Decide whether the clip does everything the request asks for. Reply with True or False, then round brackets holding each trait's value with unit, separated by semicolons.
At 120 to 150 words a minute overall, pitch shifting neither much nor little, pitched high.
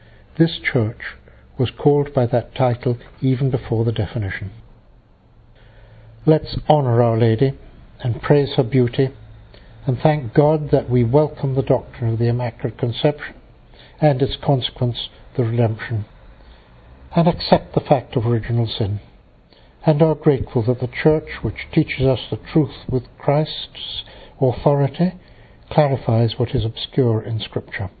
False (135 wpm; 4.1 semitones; 125 Hz)